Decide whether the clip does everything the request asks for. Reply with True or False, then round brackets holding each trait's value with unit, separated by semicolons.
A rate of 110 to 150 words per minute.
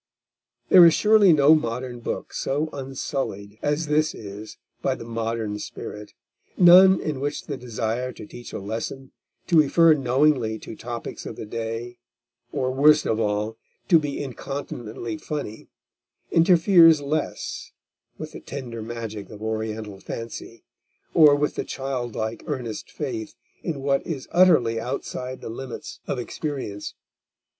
True (140 wpm)